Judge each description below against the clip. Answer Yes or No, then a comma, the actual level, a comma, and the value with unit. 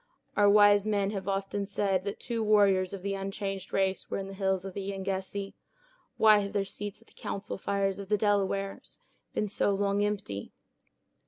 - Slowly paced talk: No, average, 185 wpm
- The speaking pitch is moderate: No, high, 200 Hz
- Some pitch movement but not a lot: No, narrow, 0.9 semitones